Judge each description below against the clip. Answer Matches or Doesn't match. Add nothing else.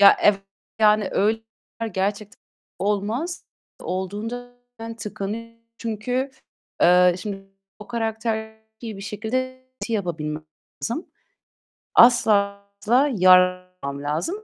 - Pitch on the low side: Doesn't match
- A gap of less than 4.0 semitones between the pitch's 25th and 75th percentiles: Matches